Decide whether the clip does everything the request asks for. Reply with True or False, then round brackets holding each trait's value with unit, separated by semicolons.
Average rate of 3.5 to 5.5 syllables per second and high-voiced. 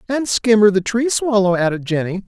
True (5.3 syllables/s; 205 Hz)